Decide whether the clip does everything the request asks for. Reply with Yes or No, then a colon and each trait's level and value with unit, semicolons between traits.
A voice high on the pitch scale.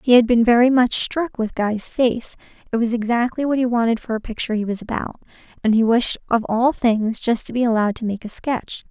Yes: high, 235 Hz